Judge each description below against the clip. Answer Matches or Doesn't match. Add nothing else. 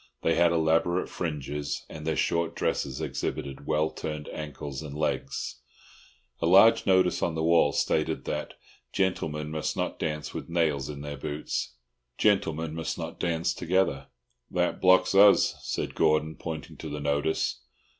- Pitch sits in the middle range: Doesn't match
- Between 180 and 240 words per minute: Doesn't match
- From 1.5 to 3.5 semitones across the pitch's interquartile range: Matches